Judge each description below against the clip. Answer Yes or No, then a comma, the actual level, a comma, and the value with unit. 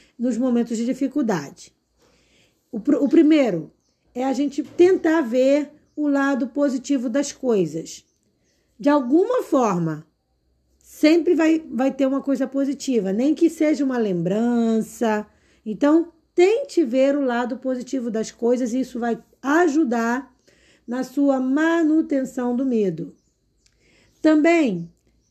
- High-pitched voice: Yes, very high, 265 Hz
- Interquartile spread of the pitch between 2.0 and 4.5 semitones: Yes, average, 4.2 semitones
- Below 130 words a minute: Yes, slow, 120 wpm